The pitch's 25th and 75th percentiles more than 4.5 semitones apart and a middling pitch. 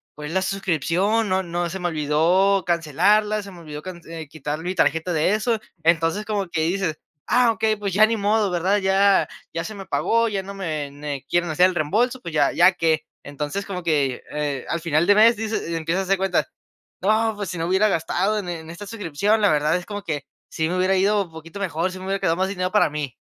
No: average, 3.8 semitones; medium, 180 Hz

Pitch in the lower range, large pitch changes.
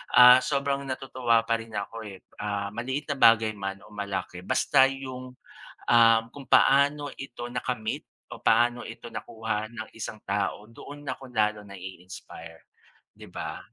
No: low, 115 Hz; average, 3.8 semitones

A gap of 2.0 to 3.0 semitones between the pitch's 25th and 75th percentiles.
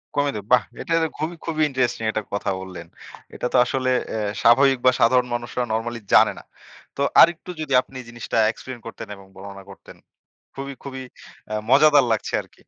No: average, 3.8 semitones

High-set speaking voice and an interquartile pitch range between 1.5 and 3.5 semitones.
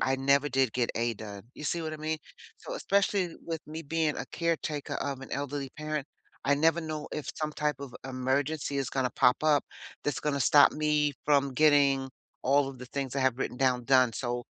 No: medium, 140 Hz; narrow, 2.6 semitones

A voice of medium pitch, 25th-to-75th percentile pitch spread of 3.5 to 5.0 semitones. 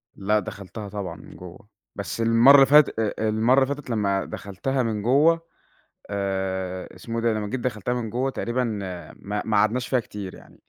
No: low, 110 Hz; average, 3.9 semitones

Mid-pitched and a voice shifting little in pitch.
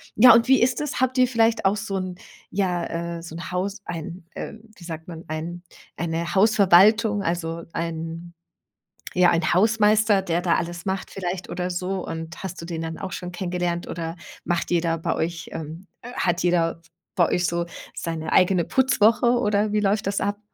No: medium, 180 Hz; average, 3.3 semitones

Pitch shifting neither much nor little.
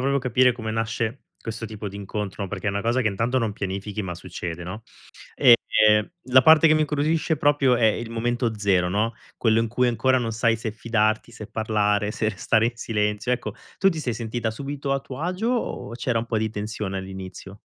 Yes: average, 3.3 semitones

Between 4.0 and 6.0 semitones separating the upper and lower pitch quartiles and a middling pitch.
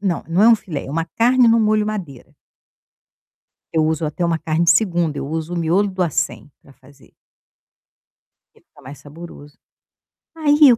Yes: wide, 5.6 semitones; medium, 170 Hz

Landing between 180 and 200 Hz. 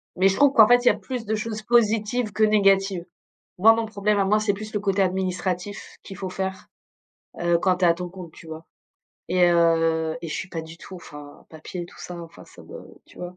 Yes: high, 190 Hz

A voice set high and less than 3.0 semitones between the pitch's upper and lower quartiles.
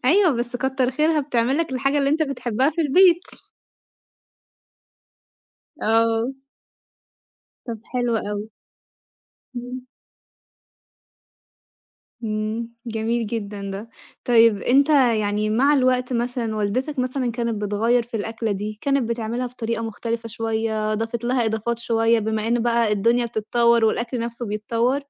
Yes: high, 235 Hz; narrow, 2.4 semitones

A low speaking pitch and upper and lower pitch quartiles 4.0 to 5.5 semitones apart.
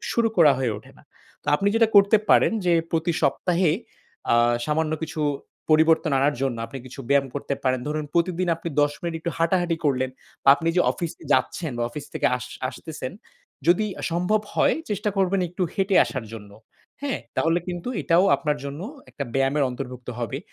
No: medium, 160 Hz; average, 4.3 semitones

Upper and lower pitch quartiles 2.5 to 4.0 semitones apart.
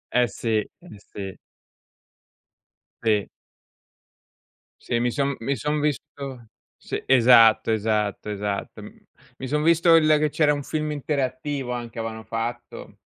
No: average, 4.5 semitones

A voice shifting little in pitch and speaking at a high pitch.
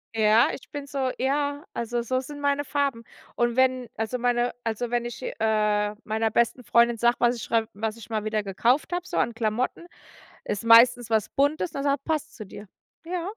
No: average, 3.8 semitones; high, 240 Hz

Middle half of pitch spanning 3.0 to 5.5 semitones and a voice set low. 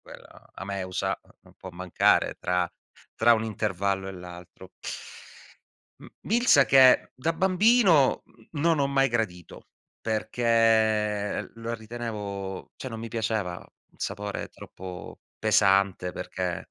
Yes: average, 4.0 semitones; low, 110 Hz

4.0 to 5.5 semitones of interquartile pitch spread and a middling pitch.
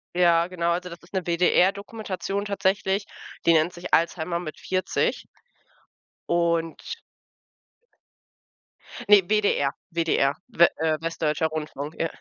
No: narrow, 2.4 semitones; medium, 170 Hz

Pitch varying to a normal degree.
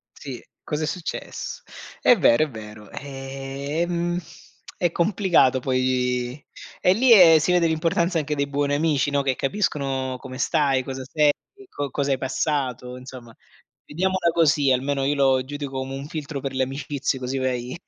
Yes: average, 3.1 semitones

